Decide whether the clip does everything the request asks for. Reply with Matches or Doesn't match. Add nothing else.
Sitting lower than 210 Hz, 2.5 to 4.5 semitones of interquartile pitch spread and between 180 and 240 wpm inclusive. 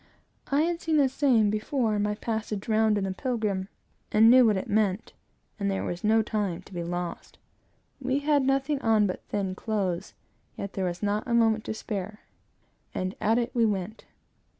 Doesn't match